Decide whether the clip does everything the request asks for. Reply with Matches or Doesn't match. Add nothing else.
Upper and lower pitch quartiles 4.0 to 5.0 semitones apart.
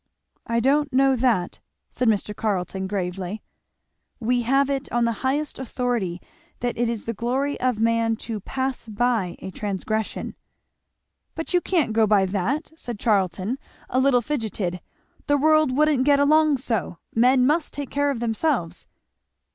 Matches